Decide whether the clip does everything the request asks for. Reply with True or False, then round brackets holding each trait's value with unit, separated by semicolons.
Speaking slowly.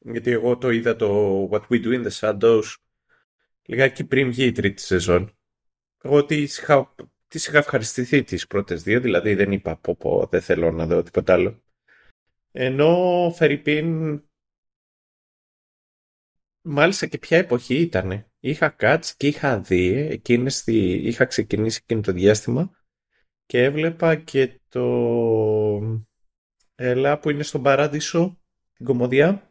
False (135 wpm)